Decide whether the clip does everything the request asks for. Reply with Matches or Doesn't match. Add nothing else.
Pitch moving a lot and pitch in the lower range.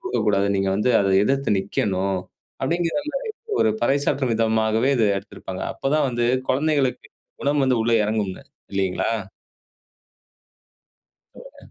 Matches